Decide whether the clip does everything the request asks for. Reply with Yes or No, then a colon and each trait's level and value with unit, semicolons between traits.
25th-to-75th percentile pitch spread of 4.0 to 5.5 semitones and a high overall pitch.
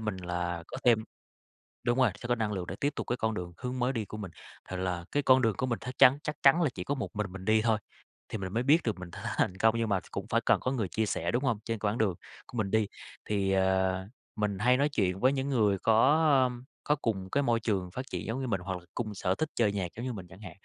No: average, 4.7 semitones; low, 110 Hz